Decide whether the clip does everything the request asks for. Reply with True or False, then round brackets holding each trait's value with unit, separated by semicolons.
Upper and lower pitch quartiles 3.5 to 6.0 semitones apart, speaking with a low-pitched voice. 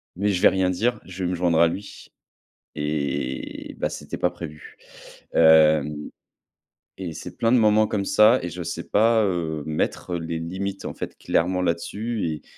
True (3.8 semitones; 90 Hz)